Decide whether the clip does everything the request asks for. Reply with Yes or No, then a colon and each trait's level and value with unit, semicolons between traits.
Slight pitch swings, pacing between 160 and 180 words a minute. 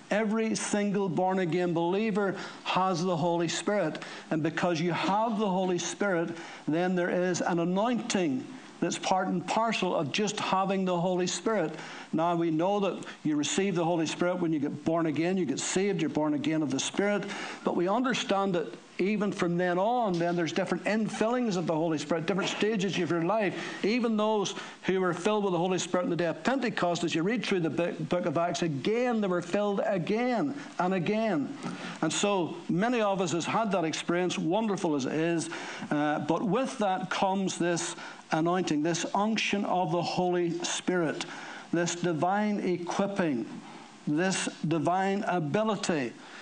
No: average, 3.1 semitones; average, 175 wpm